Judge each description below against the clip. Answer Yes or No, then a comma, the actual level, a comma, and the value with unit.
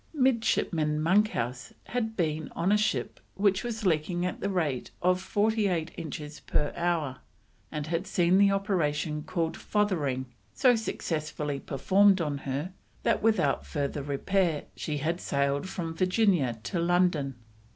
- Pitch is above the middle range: No, medium, 170 Hz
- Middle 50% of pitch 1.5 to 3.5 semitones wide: No, average, 4.9 semitones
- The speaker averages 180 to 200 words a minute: No, average, 140 wpm